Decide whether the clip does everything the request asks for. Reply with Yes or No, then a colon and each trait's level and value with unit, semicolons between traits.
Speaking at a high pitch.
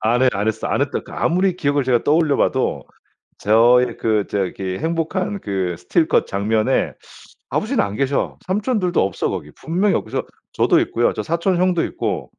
No: low, 135 Hz